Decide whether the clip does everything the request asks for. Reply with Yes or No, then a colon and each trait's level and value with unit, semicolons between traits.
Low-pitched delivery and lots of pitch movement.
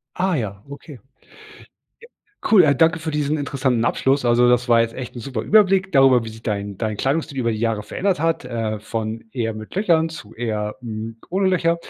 Yes: low, 125 Hz; wide, 6.1 semitones